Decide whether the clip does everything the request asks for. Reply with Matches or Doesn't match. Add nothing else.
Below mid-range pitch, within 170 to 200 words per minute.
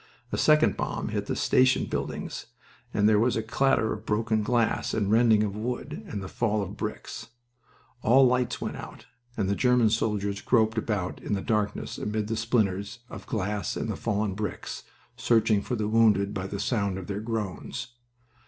Matches